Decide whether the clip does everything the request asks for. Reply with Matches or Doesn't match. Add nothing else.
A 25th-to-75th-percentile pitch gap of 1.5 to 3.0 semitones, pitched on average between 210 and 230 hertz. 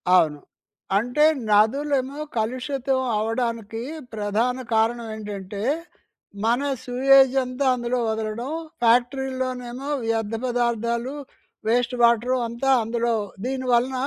Doesn't match